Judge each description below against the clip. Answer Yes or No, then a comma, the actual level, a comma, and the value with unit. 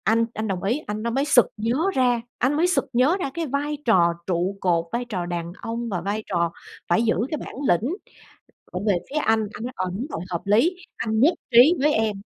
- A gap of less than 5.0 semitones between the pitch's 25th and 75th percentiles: No, average, 5.3 semitones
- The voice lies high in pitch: Yes, high, 225 Hz